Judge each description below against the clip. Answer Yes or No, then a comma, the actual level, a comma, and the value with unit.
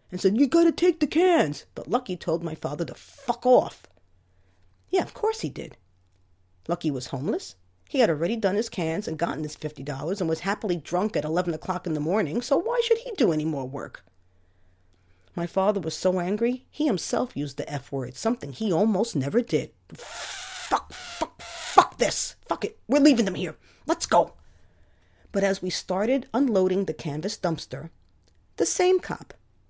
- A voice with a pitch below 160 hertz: No, medium, 170 Hz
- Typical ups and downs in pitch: No, wide, 8.7 semitones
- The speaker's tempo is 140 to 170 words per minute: No, average, 185 wpm